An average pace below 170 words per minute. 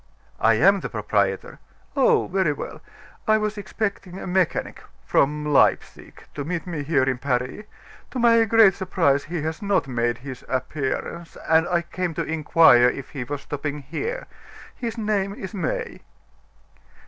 Yes: average, 155 wpm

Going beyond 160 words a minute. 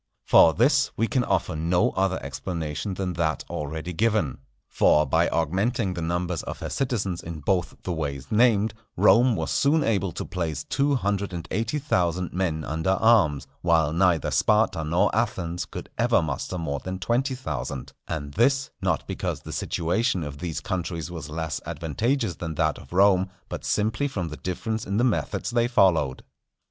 Yes: average, 175 wpm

